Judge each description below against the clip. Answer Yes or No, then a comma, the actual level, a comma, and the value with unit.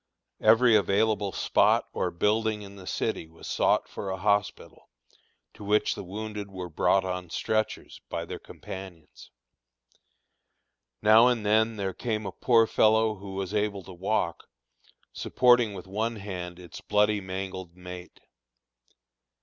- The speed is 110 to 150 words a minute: Yes, average, 140 wpm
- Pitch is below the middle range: Yes, low, 100 Hz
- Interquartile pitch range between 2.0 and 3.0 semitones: Yes, narrow, 2.6 semitones